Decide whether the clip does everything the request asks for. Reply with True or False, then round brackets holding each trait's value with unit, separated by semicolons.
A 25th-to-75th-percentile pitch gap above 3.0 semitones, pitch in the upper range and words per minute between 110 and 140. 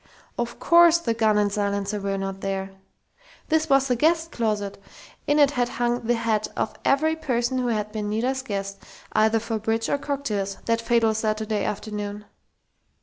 False (3.7 semitones; 225 Hz; 170 wpm)